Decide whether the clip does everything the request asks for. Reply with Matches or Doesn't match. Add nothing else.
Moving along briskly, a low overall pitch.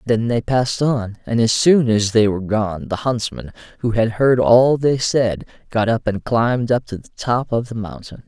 Matches